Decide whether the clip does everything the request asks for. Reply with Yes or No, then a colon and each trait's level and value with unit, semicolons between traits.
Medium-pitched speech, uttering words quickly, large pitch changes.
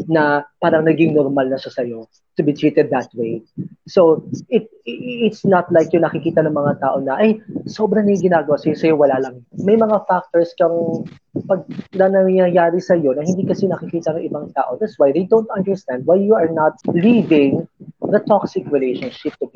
No: medium, 170 Hz; fast, 185 wpm; average, 4.5 semitones